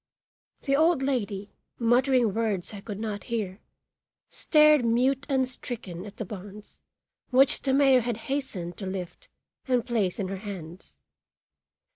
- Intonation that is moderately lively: Yes, average, 5.0 semitones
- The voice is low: No, high, 230 Hz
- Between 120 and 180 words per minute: Yes, average, 140 wpm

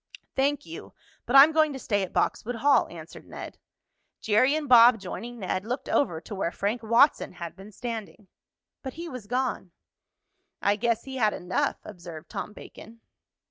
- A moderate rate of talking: Yes, average, 170 wpm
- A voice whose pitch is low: No, high, 230 Hz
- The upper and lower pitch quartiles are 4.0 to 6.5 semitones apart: Yes, average, 4.9 semitones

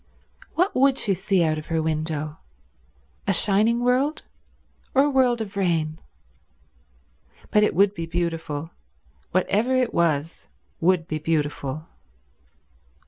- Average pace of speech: No, slow, 125 wpm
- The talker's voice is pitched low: No, medium, 175 Hz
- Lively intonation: Yes, wide, 6.1 semitones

